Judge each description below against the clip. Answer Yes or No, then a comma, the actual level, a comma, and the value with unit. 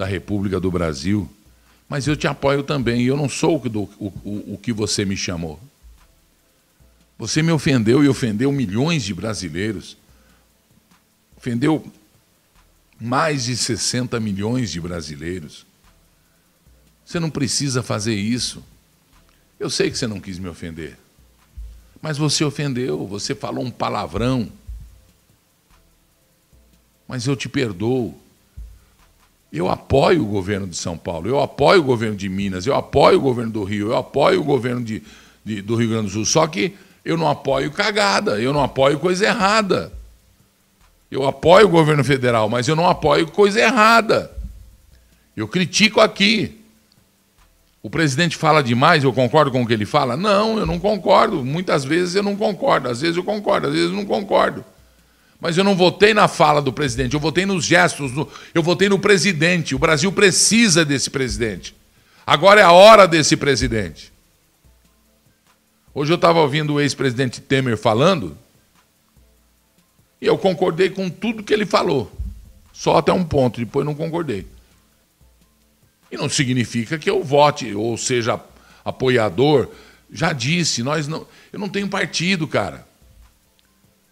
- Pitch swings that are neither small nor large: No, wide, 7.8 semitones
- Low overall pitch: Yes, low, 130 Hz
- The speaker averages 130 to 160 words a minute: Yes, average, 150 wpm